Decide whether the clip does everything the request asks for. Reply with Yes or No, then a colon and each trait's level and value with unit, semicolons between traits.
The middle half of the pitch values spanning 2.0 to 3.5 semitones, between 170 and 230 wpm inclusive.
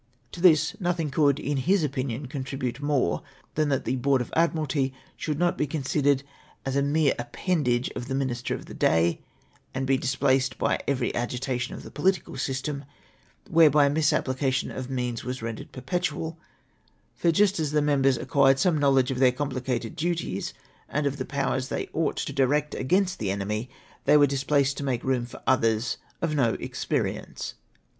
Yes: average, 2.7 semitones; average, 180 wpm